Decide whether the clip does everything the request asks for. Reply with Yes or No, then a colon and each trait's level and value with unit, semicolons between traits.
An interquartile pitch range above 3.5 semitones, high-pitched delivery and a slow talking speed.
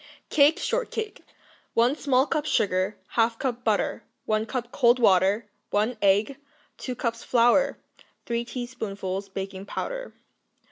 Yes: average, 4.1 semitones; high, 235 Hz; slow, 125 wpm